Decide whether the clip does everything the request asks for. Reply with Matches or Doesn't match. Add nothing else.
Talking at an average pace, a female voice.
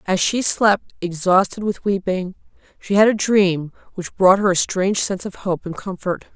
Matches